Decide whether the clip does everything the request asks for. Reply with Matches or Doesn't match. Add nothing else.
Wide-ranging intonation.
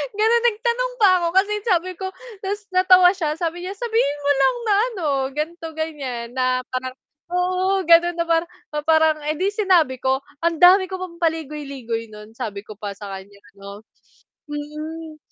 Matches